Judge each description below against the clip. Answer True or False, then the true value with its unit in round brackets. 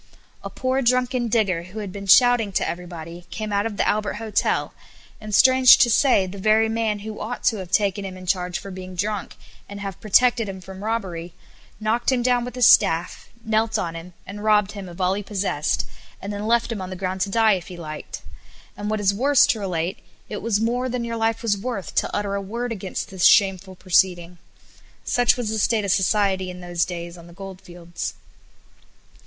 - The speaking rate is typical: False (210 wpm)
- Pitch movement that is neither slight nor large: True (3.5 semitones)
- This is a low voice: False (200 Hz)